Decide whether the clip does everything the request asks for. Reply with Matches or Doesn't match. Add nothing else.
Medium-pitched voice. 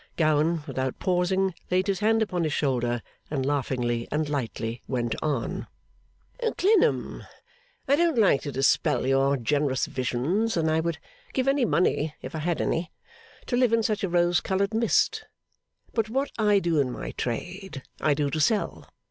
Matches